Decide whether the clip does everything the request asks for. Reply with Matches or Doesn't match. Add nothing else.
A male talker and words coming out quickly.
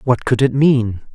Matches